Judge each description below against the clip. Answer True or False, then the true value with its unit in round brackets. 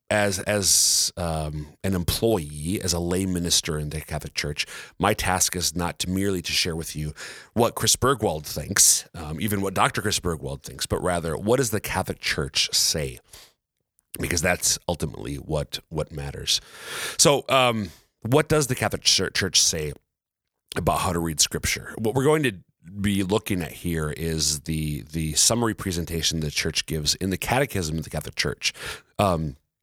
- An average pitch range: True (4.8 semitones)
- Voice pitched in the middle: False (85 Hz)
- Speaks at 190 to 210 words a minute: False (175 wpm)